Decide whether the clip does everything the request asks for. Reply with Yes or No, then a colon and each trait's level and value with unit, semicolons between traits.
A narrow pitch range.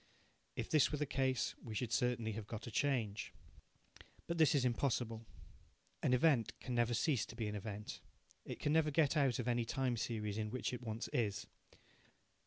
No: average, 3.6 semitones